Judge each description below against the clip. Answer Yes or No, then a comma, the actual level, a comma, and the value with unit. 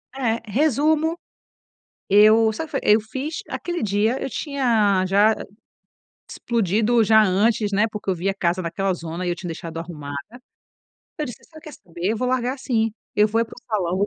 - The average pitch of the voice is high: Yes, high, 215 Hz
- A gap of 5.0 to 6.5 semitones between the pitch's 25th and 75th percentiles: No, average, 4.4 semitones